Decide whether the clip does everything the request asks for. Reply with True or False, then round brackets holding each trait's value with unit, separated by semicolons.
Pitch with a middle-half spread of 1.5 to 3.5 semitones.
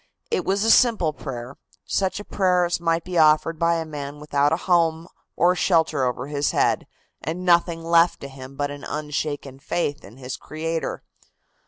True (3.2 semitones)